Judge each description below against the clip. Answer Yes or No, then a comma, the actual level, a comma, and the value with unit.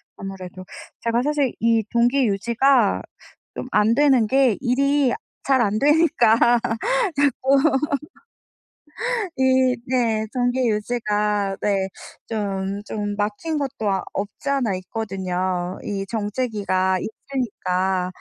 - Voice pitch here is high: Yes, high, 230 Hz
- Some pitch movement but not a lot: Yes, average, 4.9 semitones